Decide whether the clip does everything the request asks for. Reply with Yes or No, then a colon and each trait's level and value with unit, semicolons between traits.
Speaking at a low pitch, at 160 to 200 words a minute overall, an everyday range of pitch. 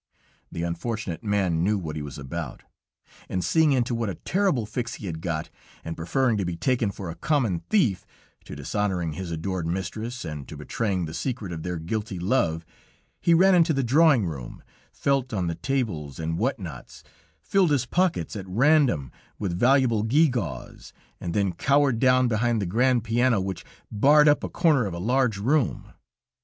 No: low, 110 Hz; average, 180 wpm; wide, 7.2 semitones